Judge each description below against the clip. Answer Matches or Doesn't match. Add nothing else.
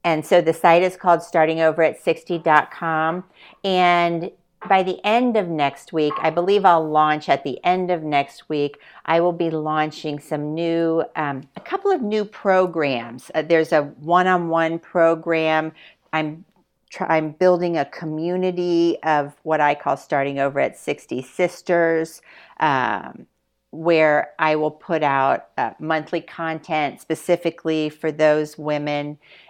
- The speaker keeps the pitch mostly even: Matches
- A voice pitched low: Doesn't match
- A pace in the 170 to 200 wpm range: Doesn't match